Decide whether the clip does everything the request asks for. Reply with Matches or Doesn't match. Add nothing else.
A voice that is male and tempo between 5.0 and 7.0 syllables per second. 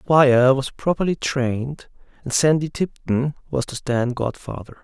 Doesn't match